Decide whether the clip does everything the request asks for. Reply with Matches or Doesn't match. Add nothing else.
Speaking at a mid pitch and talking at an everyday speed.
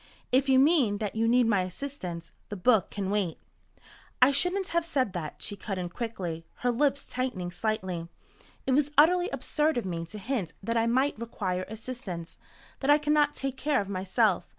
Doesn't match